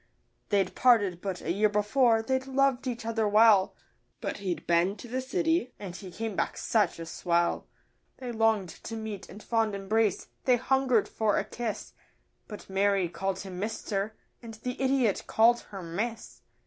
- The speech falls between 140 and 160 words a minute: No, average, 170 wpm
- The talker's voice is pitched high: Yes, high, 215 Hz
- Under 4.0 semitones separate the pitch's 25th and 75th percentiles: Yes, average, 3.5 semitones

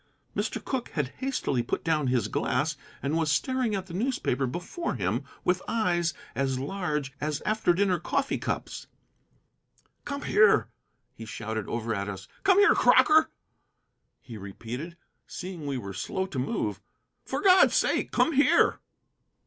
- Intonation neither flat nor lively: No, wide, 9.0 semitones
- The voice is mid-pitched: Yes, medium, 160 Hz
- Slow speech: No, average, 150 wpm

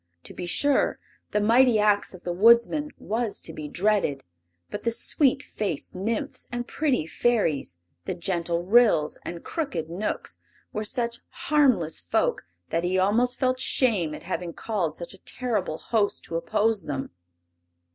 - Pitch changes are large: Yes, wide, 5.8 semitones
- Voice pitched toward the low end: No, high, 205 Hz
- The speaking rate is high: No, average, 155 wpm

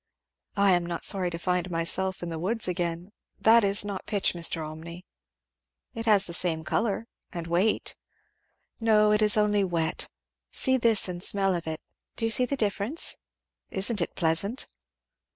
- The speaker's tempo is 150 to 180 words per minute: Yes, average, 170 wpm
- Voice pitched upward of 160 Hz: Yes, high, 190 Hz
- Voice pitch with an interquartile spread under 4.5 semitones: Yes, average, 3.7 semitones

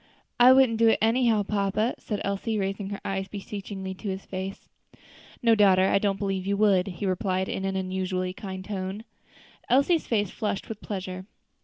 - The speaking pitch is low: No, high, 195 Hz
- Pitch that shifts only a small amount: Yes, narrow, 2.1 semitones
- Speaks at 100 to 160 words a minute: No, average, 180 wpm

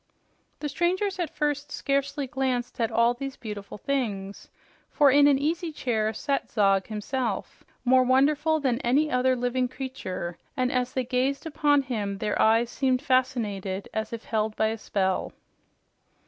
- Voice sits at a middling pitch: No, very high, 255 Hz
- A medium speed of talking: Yes, average, 155 wpm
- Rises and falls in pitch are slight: No, average, 4.2 semitones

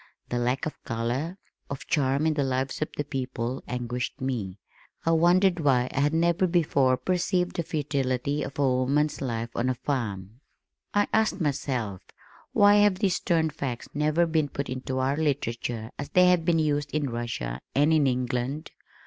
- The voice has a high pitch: No, medium, 140 Hz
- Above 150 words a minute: Yes, average, 170 wpm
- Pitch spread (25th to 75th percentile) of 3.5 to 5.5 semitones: Yes, average, 4.1 semitones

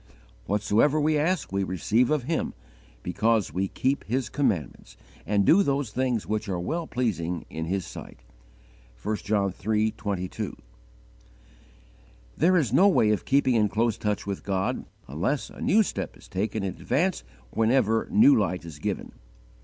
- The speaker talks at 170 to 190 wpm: No, average, 155 wpm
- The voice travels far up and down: Yes, wide, 5.8 semitones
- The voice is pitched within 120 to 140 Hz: No, low, 110 Hz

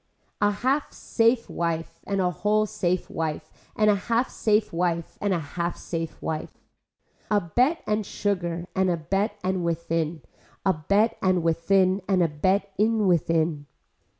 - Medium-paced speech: Yes, average, 155 wpm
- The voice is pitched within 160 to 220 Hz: Yes, medium, 185 Hz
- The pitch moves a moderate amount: Yes, average, 3.8 semitones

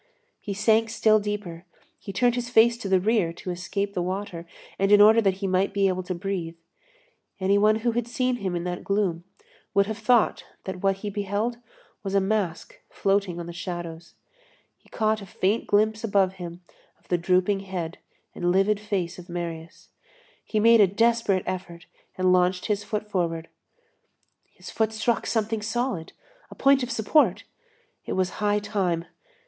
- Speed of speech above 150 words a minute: Yes, average, 175 wpm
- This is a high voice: Yes, high, 200 Hz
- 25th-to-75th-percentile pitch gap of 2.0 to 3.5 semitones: Yes, average, 3.2 semitones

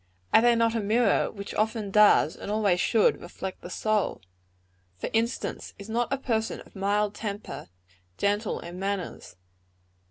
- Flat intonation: Yes, narrow, 2.1 semitones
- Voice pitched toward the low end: No, high, 210 Hz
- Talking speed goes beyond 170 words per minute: No, average, 155 wpm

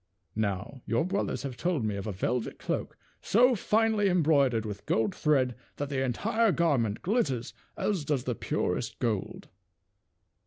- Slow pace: No, average, 150 wpm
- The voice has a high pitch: No, medium, 140 Hz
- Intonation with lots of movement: Yes, wide, 8.2 semitones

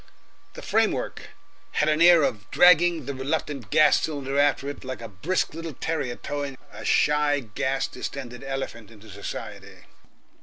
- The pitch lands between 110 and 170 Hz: Yes, medium, 140 Hz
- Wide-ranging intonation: No, average, 3.2 semitones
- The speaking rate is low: No, average, 150 wpm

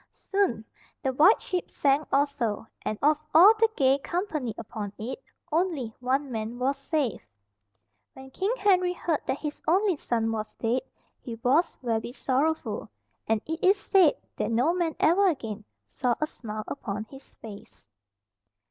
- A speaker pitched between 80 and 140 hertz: No, very high, 275 Hz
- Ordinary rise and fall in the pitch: No, wide, 6.4 semitones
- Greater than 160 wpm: No, average, 155 wpm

